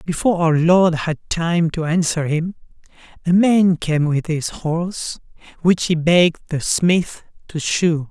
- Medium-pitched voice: Yes, medium, 165 Hz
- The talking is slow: No, average, 155 wpm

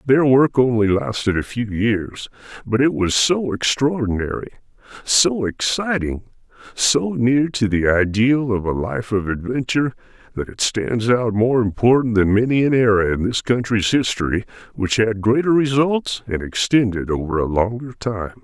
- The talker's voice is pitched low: Yes, low, 115 Hz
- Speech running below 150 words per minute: No, average, 155 wpm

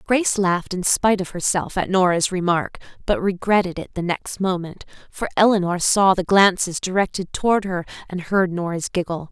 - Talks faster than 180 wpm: No, average, 175 wpm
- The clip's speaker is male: No, female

